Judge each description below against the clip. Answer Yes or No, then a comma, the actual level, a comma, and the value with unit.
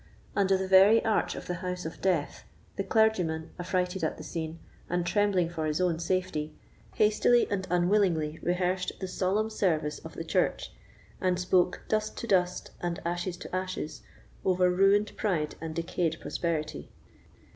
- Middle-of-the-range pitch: Yes, medium, 180 Hz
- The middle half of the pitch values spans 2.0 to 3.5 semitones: Yes, narrow, 2.6 semitones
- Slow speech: No, average, 155 wpm